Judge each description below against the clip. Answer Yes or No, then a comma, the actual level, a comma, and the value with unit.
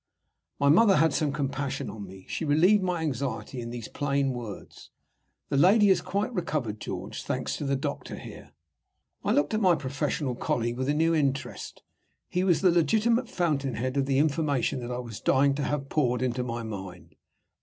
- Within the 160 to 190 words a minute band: Yes, average, 185 wpm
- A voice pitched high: No, medium, 140 Hz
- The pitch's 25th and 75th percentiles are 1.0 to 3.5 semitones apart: No, average, 4.7 semitones